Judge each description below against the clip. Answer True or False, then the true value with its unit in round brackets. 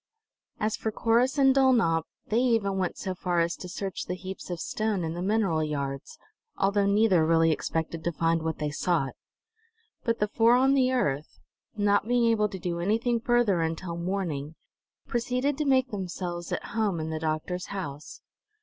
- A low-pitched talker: False (190 Hz)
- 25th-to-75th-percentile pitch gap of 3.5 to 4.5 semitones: False (5.5 semitones)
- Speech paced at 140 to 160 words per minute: False (175 wpm)